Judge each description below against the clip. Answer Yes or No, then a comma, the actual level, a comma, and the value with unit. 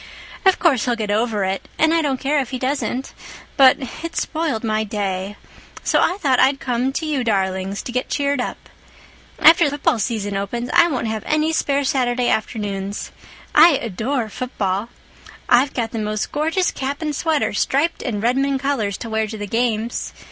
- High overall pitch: Yes, very high, 250 Hz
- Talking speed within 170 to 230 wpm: Yes, average, 175 wpm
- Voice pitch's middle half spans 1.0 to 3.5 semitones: No, average, 4.8 semitones